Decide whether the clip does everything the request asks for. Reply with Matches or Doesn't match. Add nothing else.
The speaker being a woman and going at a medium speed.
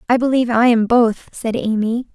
Matches